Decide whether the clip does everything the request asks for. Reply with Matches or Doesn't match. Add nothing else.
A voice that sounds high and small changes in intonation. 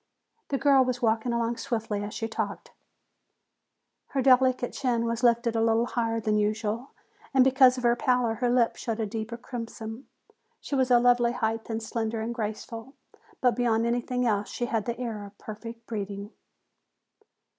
Matches